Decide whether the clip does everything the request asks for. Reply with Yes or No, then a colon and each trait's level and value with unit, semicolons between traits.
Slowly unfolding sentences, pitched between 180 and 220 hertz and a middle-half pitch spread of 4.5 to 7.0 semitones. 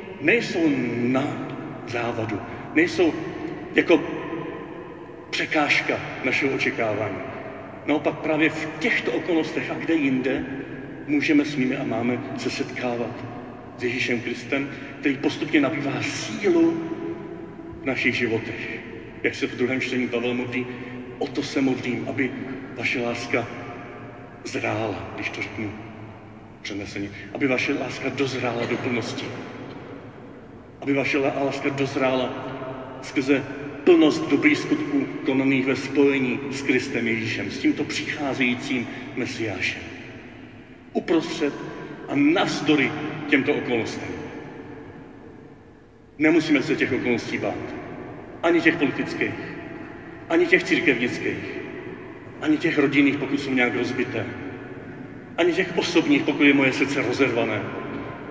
No: slow, 110 wpm; low, 135 Hz; average, 4.9 semitones